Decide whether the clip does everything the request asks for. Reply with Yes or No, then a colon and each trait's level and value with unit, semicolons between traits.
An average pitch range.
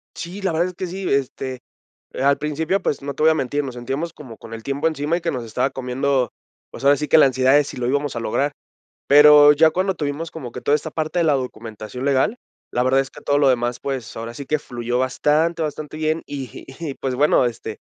Yes: average, 3.4 semitones